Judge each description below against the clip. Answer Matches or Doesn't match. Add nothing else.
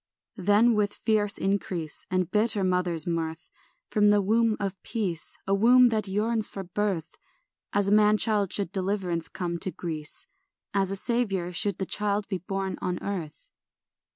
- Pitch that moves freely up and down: Doesn't match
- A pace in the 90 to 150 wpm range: Doesn't match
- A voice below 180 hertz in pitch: Doesn't match